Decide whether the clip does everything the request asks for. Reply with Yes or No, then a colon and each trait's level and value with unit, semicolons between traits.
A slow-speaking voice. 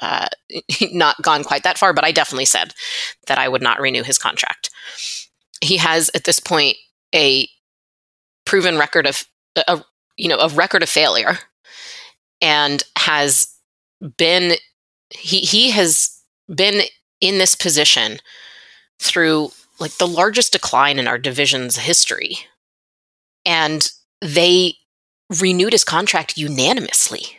Yes: slow, 125 wpm